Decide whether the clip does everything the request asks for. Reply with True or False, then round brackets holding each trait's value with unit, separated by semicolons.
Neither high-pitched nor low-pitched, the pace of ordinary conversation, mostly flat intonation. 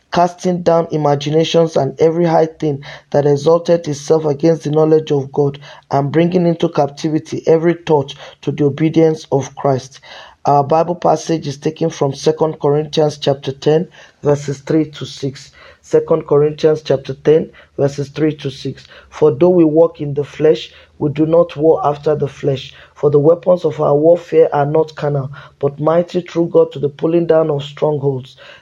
True (155 Hz; 170 wpm; 2.2 semitones)